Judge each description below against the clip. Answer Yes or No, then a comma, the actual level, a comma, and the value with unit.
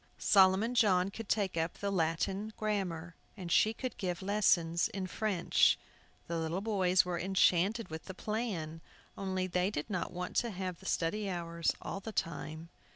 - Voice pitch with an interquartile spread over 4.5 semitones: No, average, 3.1 semitones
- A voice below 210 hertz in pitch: Yes, medium, 185 Hz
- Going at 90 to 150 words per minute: No, average, 165 wpm